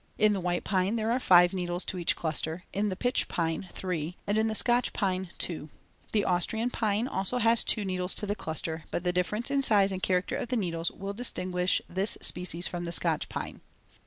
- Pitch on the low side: No, medium, 185 Hz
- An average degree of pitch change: Yes, average, 3.3 semitones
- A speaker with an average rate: No, fast, 215 wpm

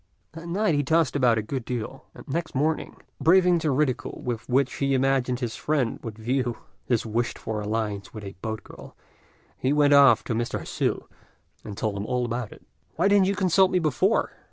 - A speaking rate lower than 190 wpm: No, average, 200 wpm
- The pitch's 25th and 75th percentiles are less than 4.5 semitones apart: No, wide, 5.6 semitones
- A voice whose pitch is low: Yes, low, 130 Hz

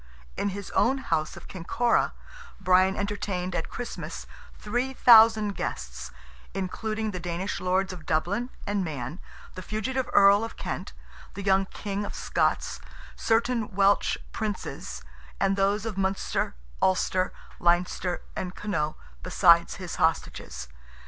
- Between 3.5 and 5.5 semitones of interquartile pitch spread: No, average, 3.0 semitones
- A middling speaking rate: No, slow, 125 wpm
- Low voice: No, high, 195 Hz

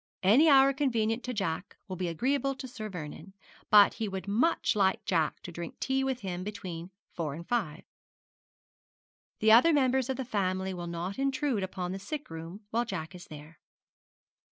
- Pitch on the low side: No, high, 200 Hz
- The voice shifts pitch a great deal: Yes, wide, 6.3 semitones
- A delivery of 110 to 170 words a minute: No, average, 180 wpm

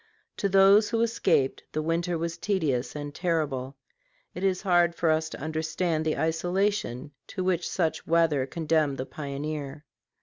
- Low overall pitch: No, medium, 160 Hz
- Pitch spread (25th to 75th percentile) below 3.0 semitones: No, average, 3.4 semitones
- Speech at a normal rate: Yes, average, 155 wpm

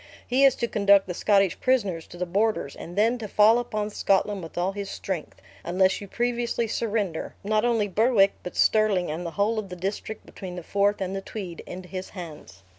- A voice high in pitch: Yes, high, 200 Hz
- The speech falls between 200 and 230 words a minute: Yes, fast, 205 wpm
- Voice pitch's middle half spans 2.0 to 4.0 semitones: Yes, average, 3.2 semitones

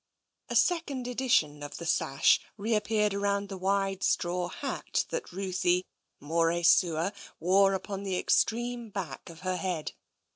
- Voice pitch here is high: Yes, high, 195 Hz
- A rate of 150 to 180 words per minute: No, average, 140 wpm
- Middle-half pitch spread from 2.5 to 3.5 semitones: Yes, average, 3.1 semitones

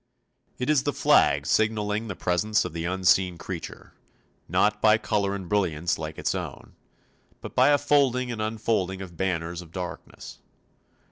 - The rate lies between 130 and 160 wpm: Yes, average, 155 wpm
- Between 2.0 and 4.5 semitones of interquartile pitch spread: Yes, average, 3.8 semitones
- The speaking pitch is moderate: No, low, 100 Hz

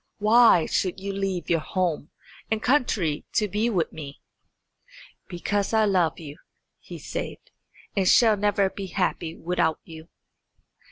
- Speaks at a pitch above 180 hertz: Yes, high, 190 Hz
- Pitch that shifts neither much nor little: Yes, average, 3.9 semitones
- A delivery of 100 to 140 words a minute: Yes, slow, 135 wpm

